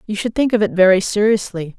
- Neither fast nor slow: No, fast, 235 wpm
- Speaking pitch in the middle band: No, high, 205 Hz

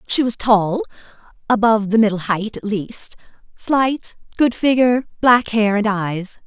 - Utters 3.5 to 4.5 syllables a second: Yes, 4.3 syllables/s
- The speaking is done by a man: No, female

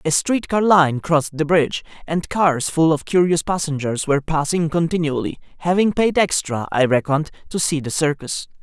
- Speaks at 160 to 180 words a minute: Yes, average, 175 wpm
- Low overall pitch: No, medium, 160 Hz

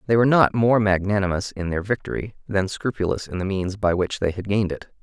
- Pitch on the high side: No, low, 100 Hz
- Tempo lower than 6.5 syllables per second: Yes, 6.0 syllables/s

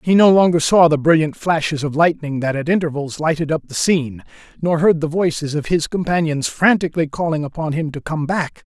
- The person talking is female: No, male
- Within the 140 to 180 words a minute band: No, fast, 205 wpm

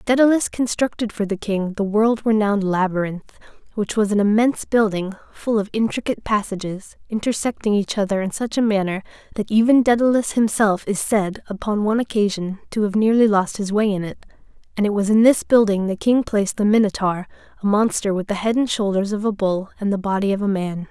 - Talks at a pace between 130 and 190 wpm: No, average, 200 wpm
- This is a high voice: Yes, high, 210 Hz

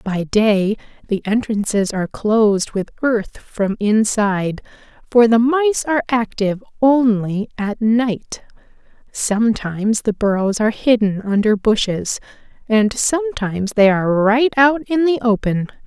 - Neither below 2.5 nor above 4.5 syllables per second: Yes, 4.3 syllables/s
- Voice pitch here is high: Yes, high, 220 Hz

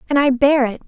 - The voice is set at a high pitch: Yes, very high, 265 Hz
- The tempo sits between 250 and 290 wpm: Yes, fast, 275 wpm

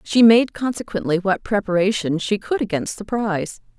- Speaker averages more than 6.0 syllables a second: No, 5.1 syllables/s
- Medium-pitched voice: No, high, 200 Hz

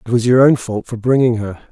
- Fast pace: Yes, fast, 280 wpm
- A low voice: Yes, low, 120 Hz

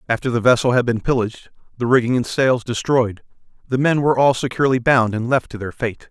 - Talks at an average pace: No, fast, 215 wpm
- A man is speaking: Yes, male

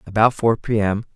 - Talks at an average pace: Yes, average, 155 wpm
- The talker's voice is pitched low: Yes, low, 110 Hz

